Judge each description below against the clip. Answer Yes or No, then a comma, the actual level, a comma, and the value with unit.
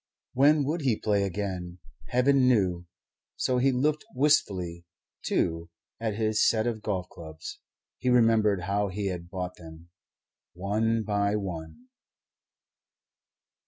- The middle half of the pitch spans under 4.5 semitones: No, average, 5.1 semitones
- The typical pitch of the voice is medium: No, low, 105 Hz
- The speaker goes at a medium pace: No, slow, 125 wpm